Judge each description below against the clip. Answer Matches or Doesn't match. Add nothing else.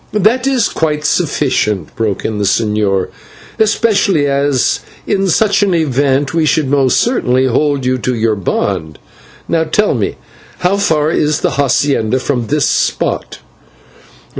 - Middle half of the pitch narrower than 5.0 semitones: Doesn't match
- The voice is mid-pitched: Matches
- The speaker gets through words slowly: Doesn't match